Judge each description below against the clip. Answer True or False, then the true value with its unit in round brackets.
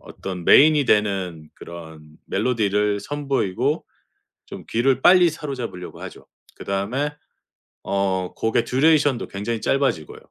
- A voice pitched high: False (110 Hz)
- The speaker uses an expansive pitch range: True (6.5 semitones)